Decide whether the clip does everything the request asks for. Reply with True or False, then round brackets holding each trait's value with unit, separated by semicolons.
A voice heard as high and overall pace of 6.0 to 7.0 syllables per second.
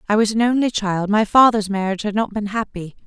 True (210 Hz; 6.1 syllables/s)